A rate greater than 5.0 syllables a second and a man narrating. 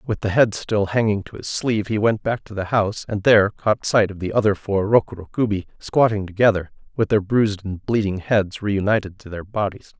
Yes: 5.5 syllables/s; male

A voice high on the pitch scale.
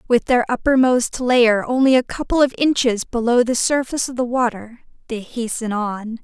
Yes: high, 240 Hz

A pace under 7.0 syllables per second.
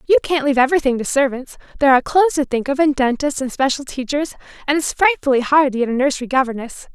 No: 7.1 syllables/s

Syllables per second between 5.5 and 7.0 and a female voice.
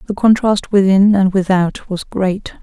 No: 4.2 syllables/s; female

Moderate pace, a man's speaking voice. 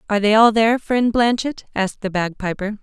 No: average, 190 wpm; female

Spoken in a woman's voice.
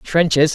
No: male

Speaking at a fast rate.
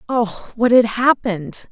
No: average, 140 wpm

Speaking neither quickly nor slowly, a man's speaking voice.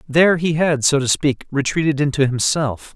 Yes: average, 185 wpm; male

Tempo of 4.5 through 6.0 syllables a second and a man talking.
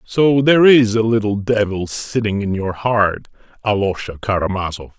Yes: 4.8 syllables/s; male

